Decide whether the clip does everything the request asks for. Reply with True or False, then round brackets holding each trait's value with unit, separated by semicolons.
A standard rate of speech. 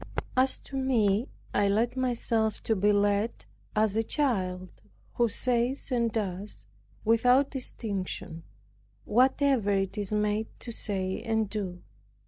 False (120 wpm)